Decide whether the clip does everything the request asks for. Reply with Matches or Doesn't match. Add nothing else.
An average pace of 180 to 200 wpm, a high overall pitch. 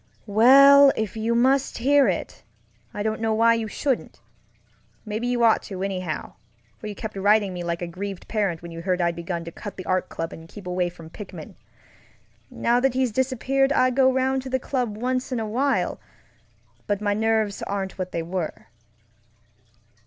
Matches